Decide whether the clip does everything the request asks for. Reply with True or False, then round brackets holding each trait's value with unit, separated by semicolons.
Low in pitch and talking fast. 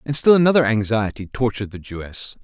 False (115 Hz; 175 wpm)